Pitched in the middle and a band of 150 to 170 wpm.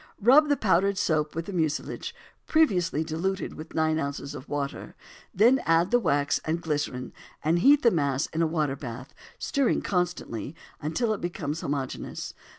Yes: medium, 160 Hz; average, 160 wpm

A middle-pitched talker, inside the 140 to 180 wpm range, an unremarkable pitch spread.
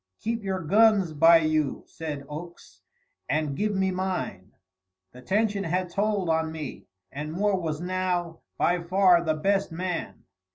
Yes: medium, 175 Hz; average, 150 wpm; average, 3.5 semitones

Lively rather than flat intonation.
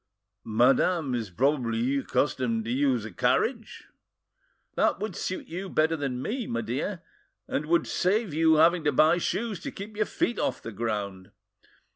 Yes: wide, 7.0 semitones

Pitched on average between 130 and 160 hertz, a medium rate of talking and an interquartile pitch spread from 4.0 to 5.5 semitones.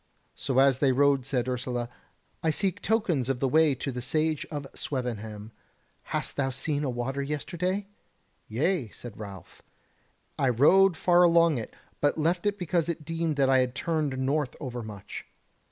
Yes: medium, 140 Hz; average, 160 wpm; average, 4.6 semitones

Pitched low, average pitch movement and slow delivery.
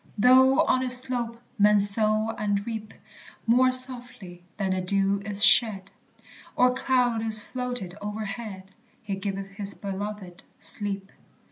No: high, 210 Hz; average, 3.7 semitones; slow, 130 wpm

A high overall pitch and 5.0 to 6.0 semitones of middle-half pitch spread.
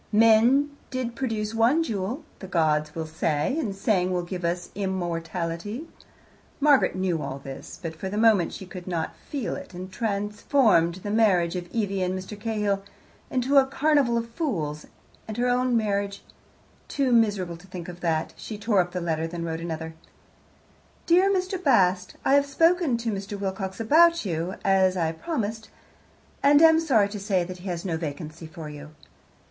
Yes: high, 195 Hz; wide, 5.4 semitones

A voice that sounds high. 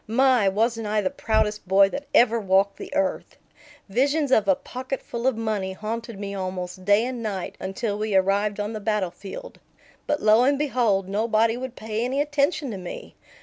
Yes: high, 215 Hz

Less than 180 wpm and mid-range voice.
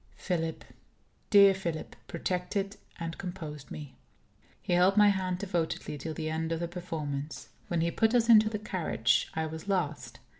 Yes: average, 160 wpm; medium, 175 Hz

